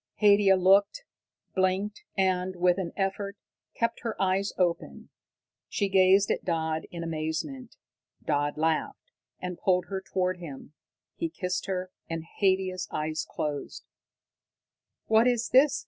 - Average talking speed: No, slow, 130 wpm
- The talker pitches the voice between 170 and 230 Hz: Yes, medium, 185 Hz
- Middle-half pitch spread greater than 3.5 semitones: No, average, 2.9 semitones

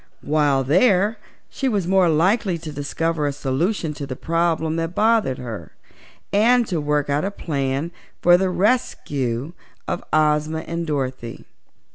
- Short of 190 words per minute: Yes, average, 145 wpm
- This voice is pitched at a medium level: Yes, medium, 160 Hz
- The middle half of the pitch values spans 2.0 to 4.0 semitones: No, average, 4.6 semitones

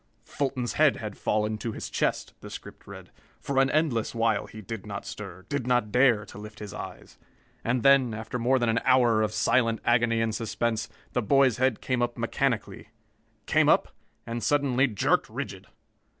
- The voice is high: No, low, 120 Hz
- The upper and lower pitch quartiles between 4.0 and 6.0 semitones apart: No, average, 2.9 semitones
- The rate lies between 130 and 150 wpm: No, average, 180 wpm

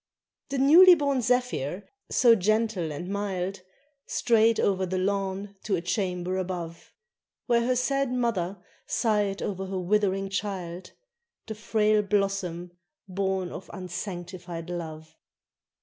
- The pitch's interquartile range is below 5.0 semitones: Yes, average, 3.3 semitones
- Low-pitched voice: No, high, 195 Hz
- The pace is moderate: No, slow, 120 wpm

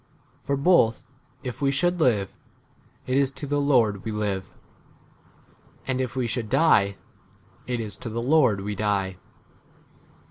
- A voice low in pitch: Yes, low, 120 Hz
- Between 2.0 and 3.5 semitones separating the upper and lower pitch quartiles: No, average, 4.9 semitones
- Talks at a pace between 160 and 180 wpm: No, average, 145 wpm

